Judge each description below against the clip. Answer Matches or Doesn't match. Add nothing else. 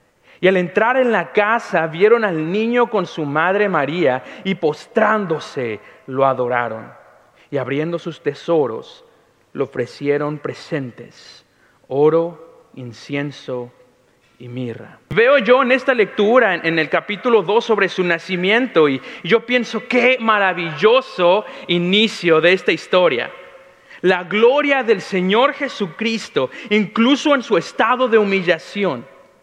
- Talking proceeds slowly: Matches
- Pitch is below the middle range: Doesn't match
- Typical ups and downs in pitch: Doesn't match